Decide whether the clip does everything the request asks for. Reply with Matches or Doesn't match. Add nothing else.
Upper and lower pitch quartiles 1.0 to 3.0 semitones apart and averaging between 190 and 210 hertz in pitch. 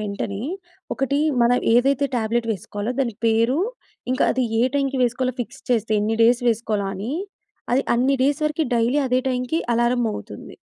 Doesn't match